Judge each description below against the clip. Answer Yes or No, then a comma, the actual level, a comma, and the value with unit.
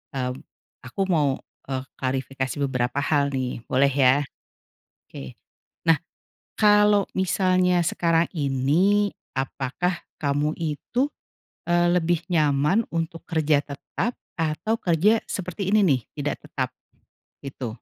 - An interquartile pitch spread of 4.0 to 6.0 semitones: Yes, average, 4.9 semitones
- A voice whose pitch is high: No, medium, 155 Hz